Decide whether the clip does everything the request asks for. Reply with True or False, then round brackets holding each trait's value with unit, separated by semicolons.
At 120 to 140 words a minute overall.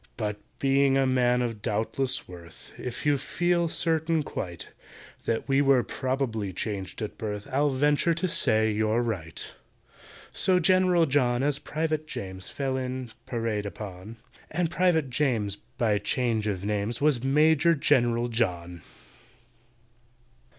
True (135 wpm)